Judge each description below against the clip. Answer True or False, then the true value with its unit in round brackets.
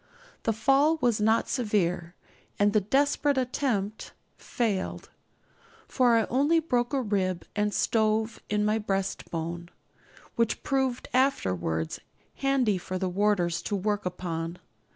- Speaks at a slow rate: True (125 wpm)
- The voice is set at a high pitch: True (210 Hz)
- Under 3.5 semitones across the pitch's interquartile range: False (5.1 semitones)